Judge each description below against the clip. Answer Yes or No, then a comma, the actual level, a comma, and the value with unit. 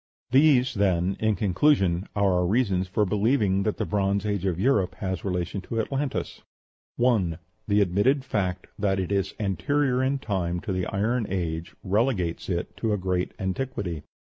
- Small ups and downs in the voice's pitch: No, average, 4.2 semitones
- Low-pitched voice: Yes, low, 100 Hz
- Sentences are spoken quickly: No, average, 180 wpm